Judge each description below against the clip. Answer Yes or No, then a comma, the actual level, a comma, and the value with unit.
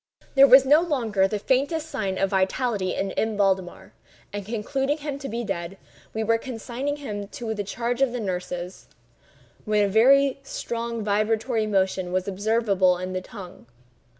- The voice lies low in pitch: No, high, 215 Hz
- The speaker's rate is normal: Yes, average, 160 wpm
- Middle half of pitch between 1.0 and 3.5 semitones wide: No, average, 4.7 semitones